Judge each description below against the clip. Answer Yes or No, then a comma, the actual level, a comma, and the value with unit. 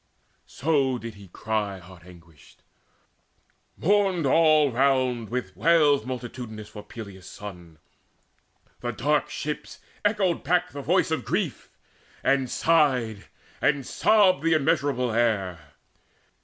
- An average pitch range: No, wide, 6.7 semitones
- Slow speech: Yes, slow, 110 wpm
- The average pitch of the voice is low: Yes, low, 125 Hz